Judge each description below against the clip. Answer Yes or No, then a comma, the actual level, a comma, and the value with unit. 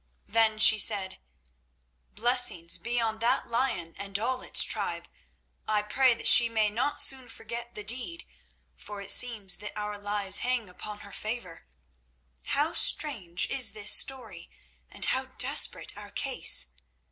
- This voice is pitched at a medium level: No, high, 220 Hz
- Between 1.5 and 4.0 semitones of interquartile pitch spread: Yes, average, 3.1 semitones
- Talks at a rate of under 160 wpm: Yes, average, 145 wpm